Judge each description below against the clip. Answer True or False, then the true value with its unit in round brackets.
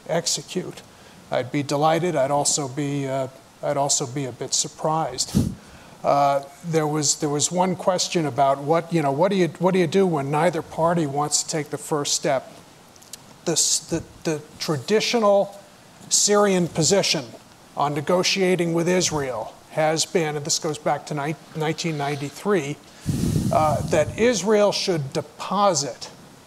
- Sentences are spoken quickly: False (145 wpm)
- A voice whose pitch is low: False (160 Hz)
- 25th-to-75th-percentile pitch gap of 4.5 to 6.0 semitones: False (3.7 semitones)